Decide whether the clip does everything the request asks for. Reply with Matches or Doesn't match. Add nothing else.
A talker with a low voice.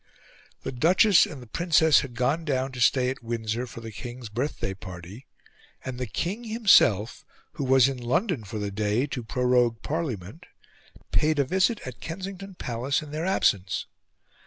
Matches